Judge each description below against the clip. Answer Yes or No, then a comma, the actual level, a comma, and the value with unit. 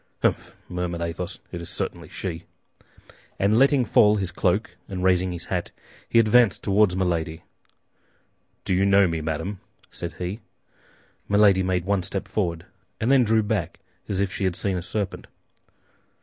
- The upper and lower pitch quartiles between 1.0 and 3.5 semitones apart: Yes, average, 2.8 semitones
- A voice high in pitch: No, very low, 95 Hz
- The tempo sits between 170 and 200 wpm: No, average, 160 wpm